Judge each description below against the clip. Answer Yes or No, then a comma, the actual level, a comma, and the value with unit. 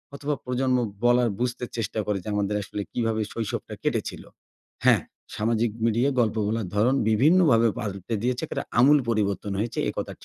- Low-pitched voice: Yes, low, 115 Hz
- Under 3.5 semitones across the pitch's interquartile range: Yes, average, 2.9 semitones